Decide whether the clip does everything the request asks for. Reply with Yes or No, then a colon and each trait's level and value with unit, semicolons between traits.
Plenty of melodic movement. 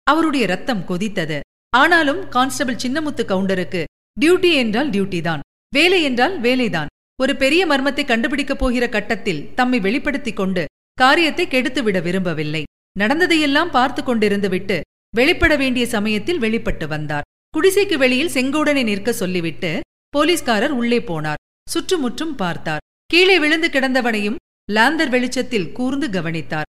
Yes: wide, 7.3 semitones